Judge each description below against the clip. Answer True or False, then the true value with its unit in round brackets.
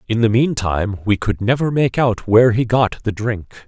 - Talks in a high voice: False (115 Hz)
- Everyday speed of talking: False (210 wpm)